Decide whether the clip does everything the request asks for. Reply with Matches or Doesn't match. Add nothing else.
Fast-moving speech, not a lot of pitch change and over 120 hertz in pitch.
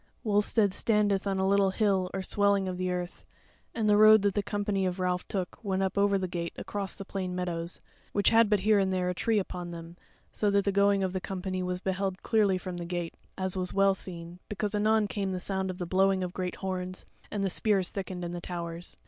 Matches